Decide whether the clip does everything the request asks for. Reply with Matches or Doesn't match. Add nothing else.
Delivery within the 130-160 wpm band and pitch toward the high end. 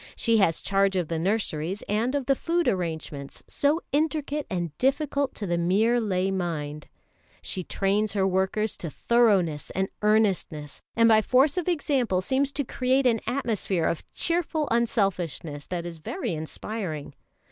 Matches